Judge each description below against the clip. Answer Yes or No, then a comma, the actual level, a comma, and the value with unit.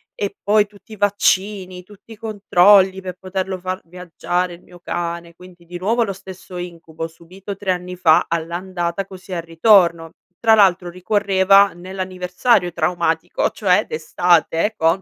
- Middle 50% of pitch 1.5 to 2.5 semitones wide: Yes, narrow, 2.2 semitones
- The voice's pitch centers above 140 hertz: Yes, medium, 185 Hz